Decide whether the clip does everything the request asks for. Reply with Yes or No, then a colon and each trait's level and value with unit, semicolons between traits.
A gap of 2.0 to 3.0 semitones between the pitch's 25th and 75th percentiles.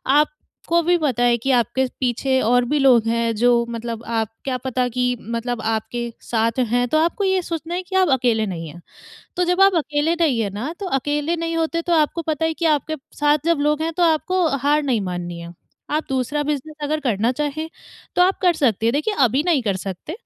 No: wide, 5.4 semitones